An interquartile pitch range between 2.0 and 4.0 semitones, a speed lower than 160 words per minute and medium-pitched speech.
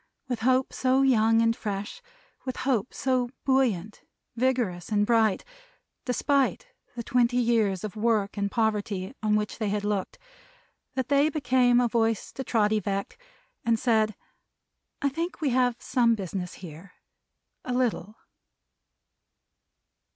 No: average, 3.6 semitones; slow, 135 wpm; high, 230 Hz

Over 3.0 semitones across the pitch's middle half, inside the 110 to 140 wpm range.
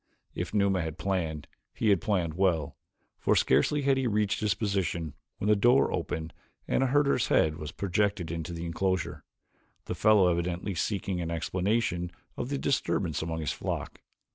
No: average, 4.2 semitones; average, 165 wpm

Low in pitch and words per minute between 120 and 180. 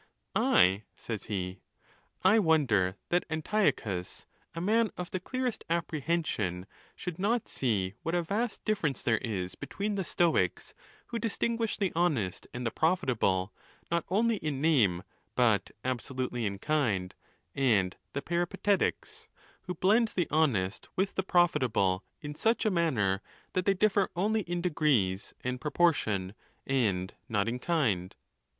No: medium, 150 Hz; average, 145 wpm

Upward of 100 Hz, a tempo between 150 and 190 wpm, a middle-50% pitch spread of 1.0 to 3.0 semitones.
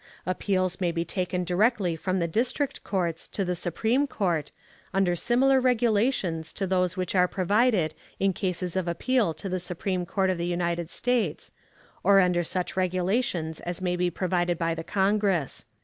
Yes: medium, 185 Hz; average, 165 wpm; narrow, 2.5 semitones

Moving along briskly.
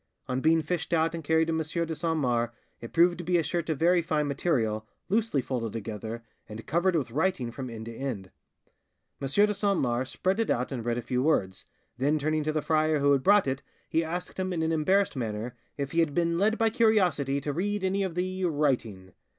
Yes: fast, 225 wpm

